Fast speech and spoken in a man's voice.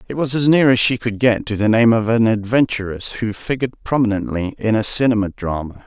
Yes: fast, 215 wpm; male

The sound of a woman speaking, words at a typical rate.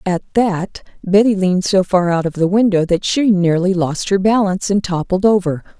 Yes: female; average, 195 wpm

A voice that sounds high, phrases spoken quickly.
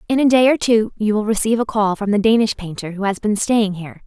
Yes: high, 215 Hz; fast, 280 wpm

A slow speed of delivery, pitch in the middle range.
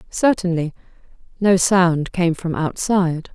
Yes: slow, 110 wpm; medium, 175 Hz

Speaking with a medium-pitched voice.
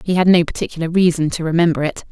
Yes: medium, 165 Hz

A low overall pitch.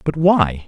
Yes: low, 130 Hz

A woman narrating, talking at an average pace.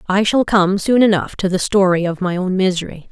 No: female; fast, 230 wpm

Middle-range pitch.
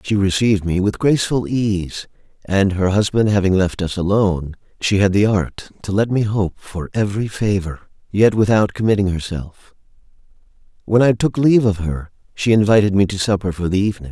No: low, 100 Hz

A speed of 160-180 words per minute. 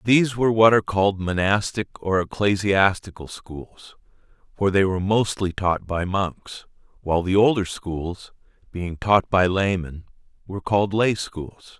No: average, 140 wpm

